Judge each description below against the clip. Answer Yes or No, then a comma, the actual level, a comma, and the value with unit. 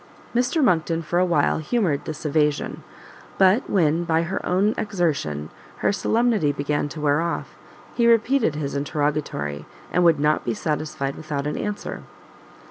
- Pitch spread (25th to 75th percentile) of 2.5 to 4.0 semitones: No, average, 4.6 semitones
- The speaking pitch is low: No, medium, 155 Hz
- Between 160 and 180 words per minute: No, average, 150 wpm